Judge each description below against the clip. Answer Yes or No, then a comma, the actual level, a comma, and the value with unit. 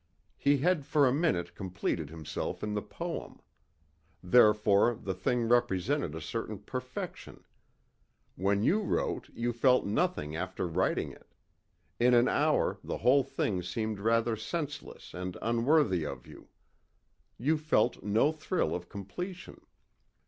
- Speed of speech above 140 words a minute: No, slow, 135 wpm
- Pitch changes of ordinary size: No, wide, 6.5 semitones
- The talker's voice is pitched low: Yes, low, 115 Hz